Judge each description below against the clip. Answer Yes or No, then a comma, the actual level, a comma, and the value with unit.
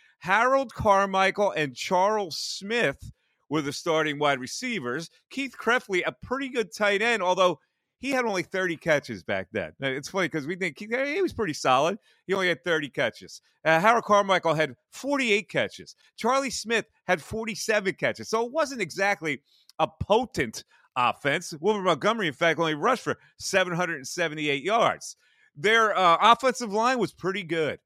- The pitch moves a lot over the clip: Yes, wide, 5.8 semitones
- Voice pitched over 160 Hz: Yes, high, 190 Hz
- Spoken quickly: No, average, 160 wpm